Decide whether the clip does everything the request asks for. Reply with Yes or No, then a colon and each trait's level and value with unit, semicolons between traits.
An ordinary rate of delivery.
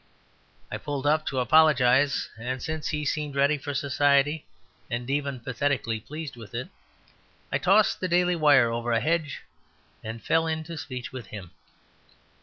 Yes: average, 155 wpm